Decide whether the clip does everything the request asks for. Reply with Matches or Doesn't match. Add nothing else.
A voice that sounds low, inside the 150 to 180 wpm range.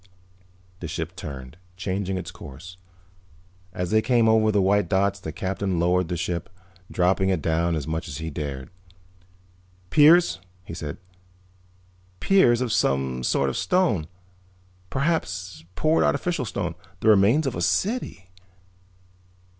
Doesn't match